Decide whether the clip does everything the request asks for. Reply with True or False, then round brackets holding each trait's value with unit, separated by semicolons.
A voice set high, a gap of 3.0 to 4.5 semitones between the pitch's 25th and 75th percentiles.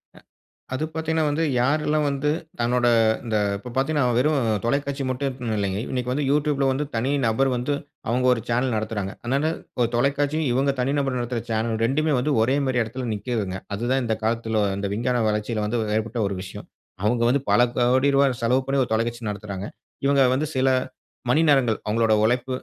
False (125 Hz; 3.5 semitones)